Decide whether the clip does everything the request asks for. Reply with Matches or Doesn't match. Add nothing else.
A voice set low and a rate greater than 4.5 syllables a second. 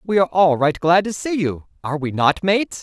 Doesn't match